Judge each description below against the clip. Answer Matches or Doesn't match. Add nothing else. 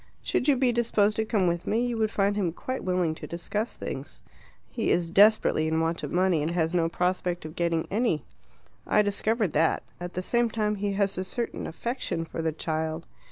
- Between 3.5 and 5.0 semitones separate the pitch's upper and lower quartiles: Matches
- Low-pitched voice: Doesn't match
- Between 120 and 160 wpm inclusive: Doesn't match